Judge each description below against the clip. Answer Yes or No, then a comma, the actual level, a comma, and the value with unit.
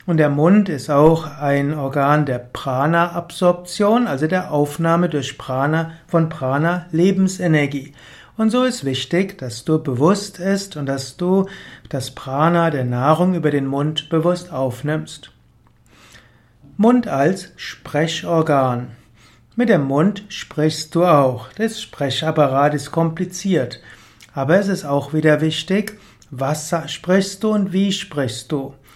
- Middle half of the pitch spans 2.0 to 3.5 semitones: No, average, 4.6 semitones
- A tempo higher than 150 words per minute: No, average, 130 wpm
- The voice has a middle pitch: Yes, medium, 155 Hz